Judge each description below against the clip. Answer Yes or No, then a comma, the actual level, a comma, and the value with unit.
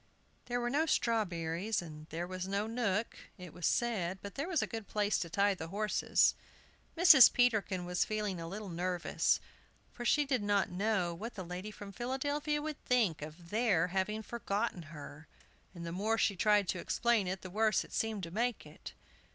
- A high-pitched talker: Yes, high, 205 Hz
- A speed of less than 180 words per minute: No, average, 190 wpm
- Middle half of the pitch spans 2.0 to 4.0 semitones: No, average, 4.4 semitones